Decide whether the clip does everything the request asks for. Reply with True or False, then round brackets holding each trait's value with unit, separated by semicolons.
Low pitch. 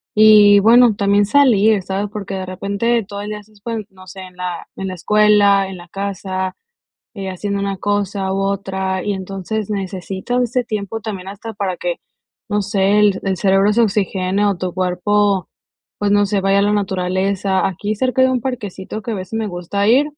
False (200 Hz)